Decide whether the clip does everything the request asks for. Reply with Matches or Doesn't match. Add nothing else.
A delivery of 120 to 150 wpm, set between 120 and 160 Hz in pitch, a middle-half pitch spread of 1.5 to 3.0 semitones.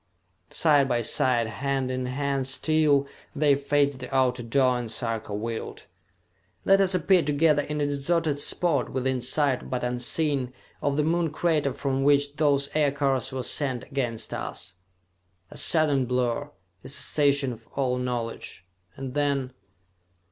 Matches